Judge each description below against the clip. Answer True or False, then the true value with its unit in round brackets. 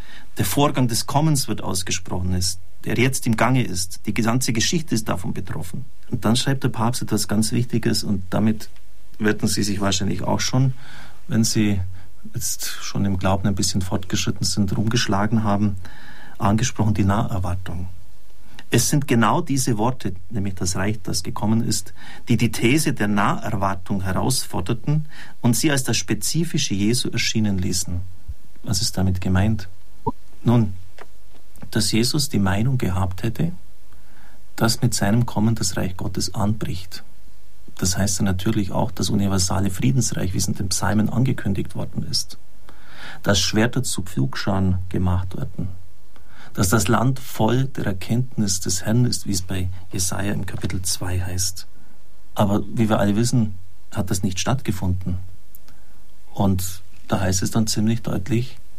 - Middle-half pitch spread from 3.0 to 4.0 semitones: True (3.6 semitones)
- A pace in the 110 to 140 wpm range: False (150 wpm)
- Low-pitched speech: True (105 Hz)